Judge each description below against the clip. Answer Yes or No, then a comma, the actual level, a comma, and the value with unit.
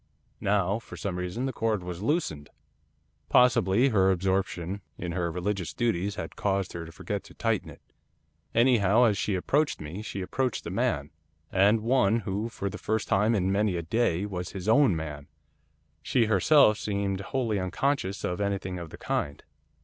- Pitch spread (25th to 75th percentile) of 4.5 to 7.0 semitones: No, average, 3.8 semitones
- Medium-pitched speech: No, low, 100 Hz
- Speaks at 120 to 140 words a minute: No, average, 170 wpm